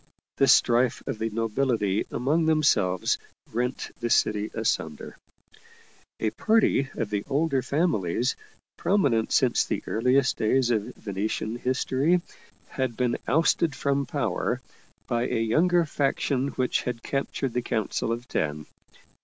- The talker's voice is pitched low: Yes, low, 125 Hz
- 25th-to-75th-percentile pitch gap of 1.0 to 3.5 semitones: No, average, 3.9 semitones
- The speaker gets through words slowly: Yes, slow, 130 wpm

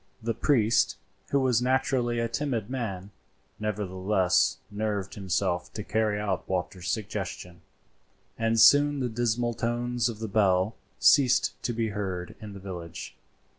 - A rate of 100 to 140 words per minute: Yes, slow, 135 wpm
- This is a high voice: No, low, 110 Hz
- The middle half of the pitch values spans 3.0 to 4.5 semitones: Yes, average, 3.8 semitones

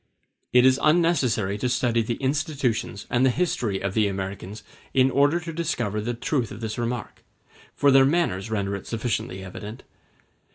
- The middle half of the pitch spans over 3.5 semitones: Yes, average, 4.7 semitones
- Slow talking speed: No, average, 165 wpm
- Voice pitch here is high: No, low, 120 Hz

